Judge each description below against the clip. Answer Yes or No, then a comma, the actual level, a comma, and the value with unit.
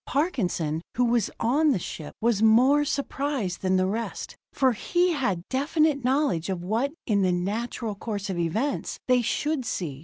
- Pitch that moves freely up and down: Yes, wide, 6.7 semitones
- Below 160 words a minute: No, average, 165 wpm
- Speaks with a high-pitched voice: Yes, high, 230 Hz